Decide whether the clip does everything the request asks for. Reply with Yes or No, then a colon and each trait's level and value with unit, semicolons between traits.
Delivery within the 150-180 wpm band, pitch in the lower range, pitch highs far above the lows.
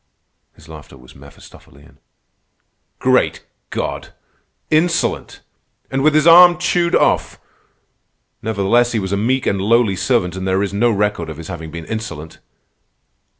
No: average, 140 wpm; low, 105 Hz; wide, 7.1 semitones